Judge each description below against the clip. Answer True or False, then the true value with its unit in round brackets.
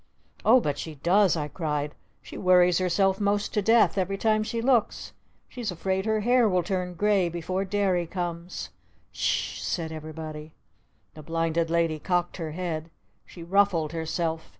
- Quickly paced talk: False (165 wpm)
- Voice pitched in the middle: True (180 Hz)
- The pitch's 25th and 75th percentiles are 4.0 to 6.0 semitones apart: False (3.6 semitones)